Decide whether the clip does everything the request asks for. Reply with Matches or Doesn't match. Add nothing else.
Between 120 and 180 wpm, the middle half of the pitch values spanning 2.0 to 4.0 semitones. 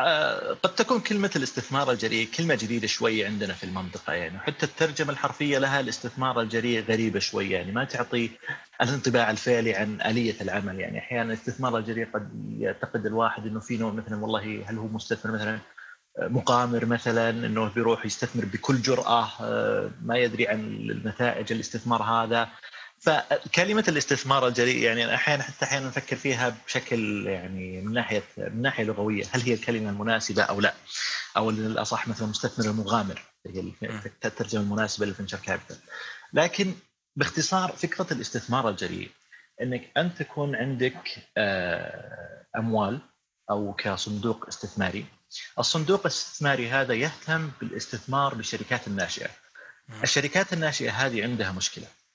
Matches